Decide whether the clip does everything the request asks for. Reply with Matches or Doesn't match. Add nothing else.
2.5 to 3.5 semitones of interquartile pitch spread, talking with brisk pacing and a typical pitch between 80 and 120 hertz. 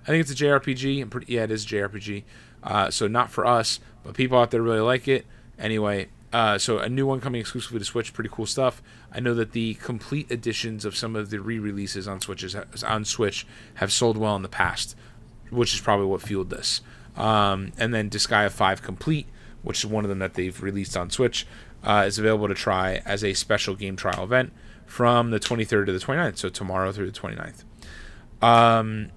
Matches